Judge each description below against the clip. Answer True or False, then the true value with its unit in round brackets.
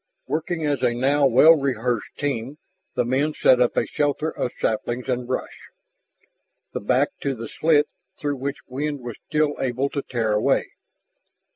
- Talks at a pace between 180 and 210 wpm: False (165 wpm)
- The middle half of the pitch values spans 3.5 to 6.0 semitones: False (3.1 semitones)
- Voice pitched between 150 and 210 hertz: False (135 Hz)